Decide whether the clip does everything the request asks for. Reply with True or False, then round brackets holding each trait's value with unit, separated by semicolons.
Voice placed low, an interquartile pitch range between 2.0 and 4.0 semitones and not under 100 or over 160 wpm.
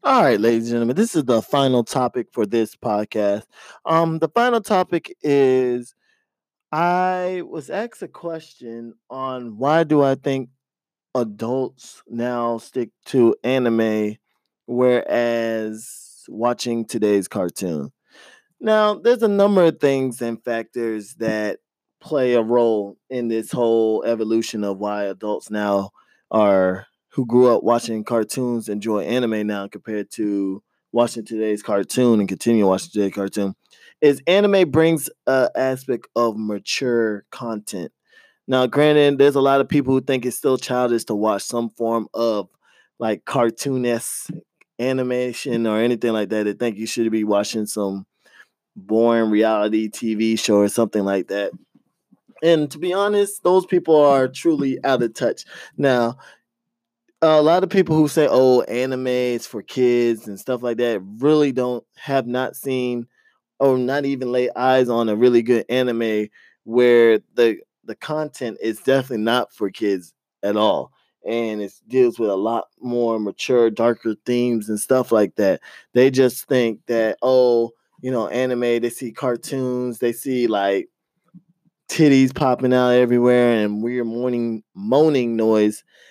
True (120 Hz; 3.1 semitones; 150 wpm)